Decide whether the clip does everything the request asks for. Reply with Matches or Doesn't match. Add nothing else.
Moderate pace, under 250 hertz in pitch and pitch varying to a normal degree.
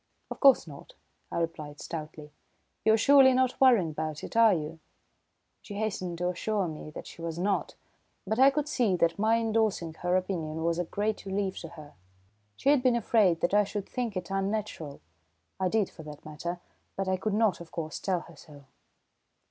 Matches